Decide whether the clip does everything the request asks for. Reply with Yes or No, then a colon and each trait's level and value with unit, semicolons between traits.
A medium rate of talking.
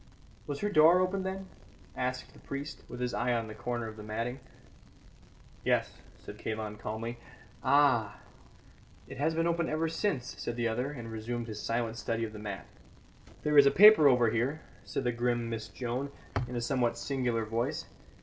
Yes: average, 180 wpm